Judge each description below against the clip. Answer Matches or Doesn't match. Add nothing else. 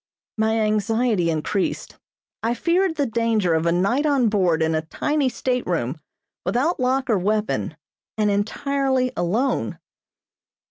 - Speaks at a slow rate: Matches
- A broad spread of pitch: Matches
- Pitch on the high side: Matches